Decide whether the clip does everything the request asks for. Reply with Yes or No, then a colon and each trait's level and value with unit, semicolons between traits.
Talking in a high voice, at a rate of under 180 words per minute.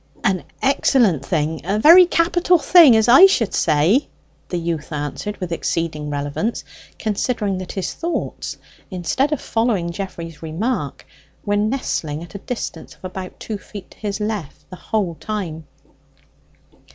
Yes: high, 195 Hz; average, 145 wpm